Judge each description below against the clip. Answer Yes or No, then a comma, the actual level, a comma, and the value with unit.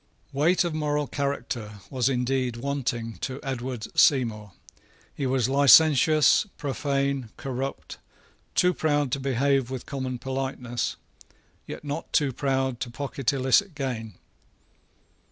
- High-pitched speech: No, low, 135 Hz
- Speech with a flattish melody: Yes, narrow, 2.2 semitones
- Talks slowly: Yes, slow, 120 wpm